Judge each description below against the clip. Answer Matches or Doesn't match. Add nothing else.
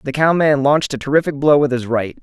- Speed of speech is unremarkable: Doesn't match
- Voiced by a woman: Doesn't match